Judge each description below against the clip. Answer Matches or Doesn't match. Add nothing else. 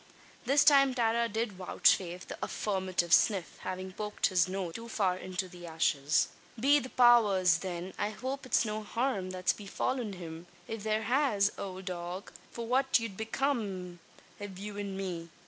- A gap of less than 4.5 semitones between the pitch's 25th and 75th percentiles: Matches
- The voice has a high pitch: Matches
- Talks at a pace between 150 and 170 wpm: Matches